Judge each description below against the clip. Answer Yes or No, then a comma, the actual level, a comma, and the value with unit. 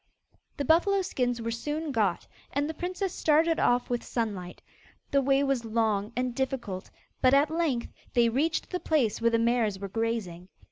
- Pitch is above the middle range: Yes, high, 245 Hz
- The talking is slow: No, average, 175 wpm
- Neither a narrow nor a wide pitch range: Yes, average, 4.7 semitones